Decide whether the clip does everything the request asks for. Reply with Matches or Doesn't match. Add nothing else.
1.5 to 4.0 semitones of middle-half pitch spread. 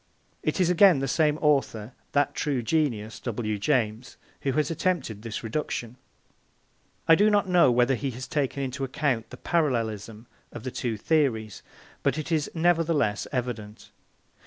Doesn't match